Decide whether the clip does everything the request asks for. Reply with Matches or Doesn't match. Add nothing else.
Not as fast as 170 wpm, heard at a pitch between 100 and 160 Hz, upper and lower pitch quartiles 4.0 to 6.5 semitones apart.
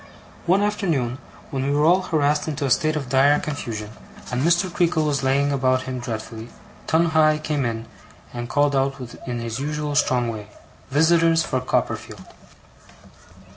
Doesn't match